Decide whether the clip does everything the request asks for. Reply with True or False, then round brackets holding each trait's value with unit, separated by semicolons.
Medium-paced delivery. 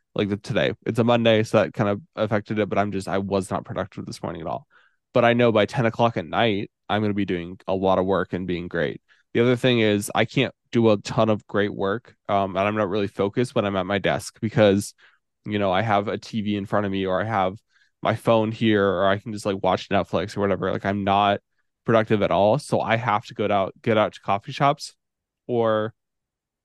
False (245 wpm)